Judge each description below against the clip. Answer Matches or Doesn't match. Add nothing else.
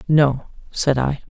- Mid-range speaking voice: Matches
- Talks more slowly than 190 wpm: Matches